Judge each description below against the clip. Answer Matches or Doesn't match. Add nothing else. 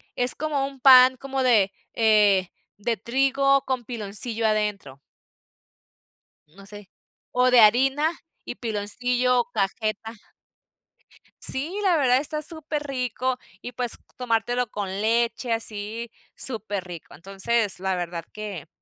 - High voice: Matches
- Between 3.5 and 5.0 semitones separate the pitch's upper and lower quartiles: Matches